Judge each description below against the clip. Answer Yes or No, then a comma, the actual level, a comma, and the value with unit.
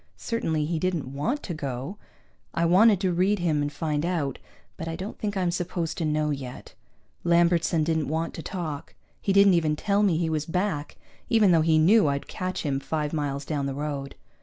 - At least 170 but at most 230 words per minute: Yes, average, 200 wpm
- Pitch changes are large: No, average, 3.5 semitones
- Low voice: No, medium, 165 Hz